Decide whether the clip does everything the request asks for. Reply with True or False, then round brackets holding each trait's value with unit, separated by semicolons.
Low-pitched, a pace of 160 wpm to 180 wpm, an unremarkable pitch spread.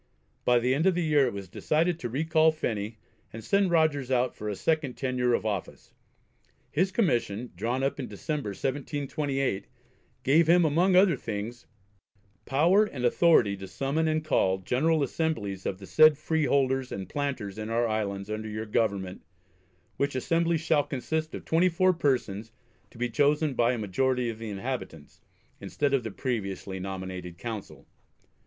False (130 Hz; 165 wpm; 6.5 semitones)